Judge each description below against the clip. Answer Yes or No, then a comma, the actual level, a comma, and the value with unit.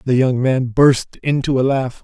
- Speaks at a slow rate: No, fast, 205 wpm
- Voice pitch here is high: No, low, 130 Hz